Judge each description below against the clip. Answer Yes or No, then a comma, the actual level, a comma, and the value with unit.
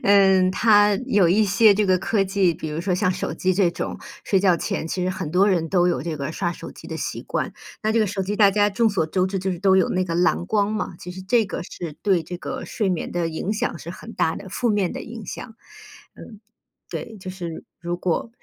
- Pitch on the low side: No, high, 190 Hz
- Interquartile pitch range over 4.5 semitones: No, average, 2.8 semitones